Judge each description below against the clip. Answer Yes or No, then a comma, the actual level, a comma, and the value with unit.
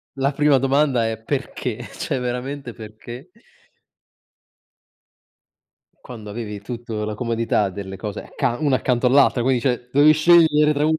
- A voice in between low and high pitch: No, low, 125 Hz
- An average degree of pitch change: Yes, average, 4.0 semitones